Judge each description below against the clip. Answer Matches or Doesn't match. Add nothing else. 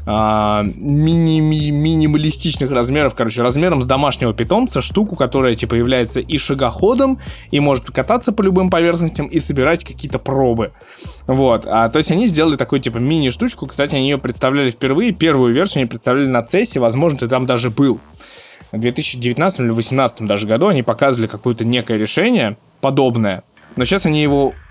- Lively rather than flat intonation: Doesn't match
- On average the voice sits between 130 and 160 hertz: Matches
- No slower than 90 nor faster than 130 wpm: Doesn't match